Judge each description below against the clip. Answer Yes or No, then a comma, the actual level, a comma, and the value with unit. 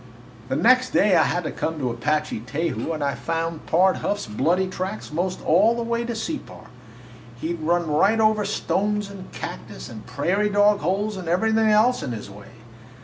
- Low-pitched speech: No, medium, 185 Hz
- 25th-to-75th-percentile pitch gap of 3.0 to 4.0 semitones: No, average, 5.3 semitones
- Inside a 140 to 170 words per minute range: No, average, 190 wpm